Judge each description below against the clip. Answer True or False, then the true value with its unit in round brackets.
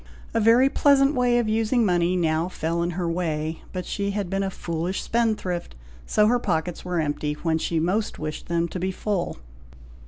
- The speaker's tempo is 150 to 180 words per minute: False (190 wpm)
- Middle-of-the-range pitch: True (180 Hz)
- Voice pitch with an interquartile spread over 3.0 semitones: True (4.4 semitones)